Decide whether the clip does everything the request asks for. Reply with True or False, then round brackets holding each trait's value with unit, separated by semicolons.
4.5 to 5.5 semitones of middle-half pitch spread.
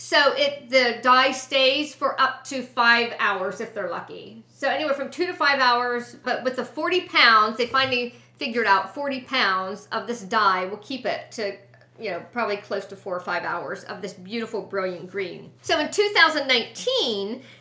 True (4.8 semitones)